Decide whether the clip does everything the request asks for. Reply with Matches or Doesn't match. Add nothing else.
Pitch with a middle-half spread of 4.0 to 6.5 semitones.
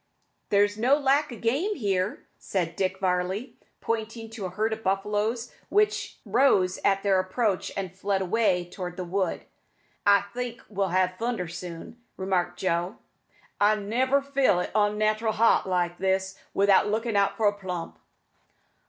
Doesn't match